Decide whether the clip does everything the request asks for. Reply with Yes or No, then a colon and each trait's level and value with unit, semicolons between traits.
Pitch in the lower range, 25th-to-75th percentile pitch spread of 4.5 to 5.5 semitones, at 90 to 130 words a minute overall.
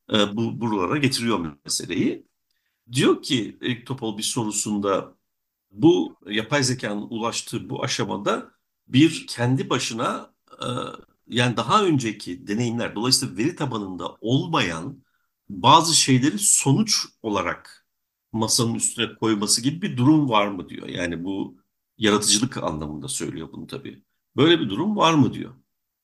No: low, 115 Hz; average, 3.4 semitones; average, 125 wpm